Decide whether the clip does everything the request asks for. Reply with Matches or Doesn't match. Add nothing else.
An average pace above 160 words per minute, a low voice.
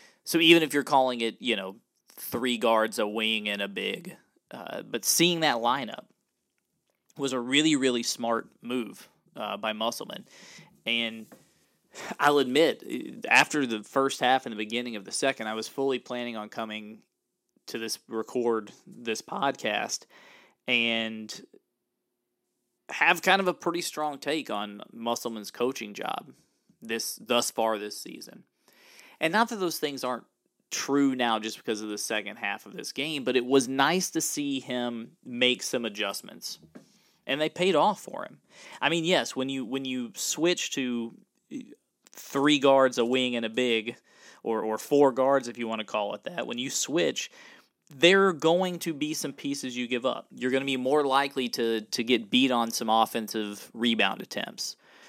Matches